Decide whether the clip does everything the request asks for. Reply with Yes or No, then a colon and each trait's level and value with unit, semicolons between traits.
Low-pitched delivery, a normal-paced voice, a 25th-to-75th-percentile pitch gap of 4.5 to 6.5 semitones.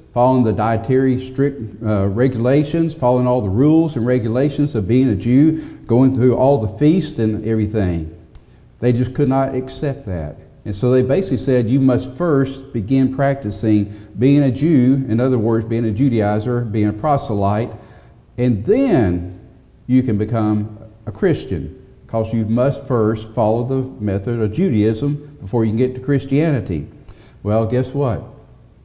No: low, 125 Hz; average, 160 wpm; average, 3.6 semitones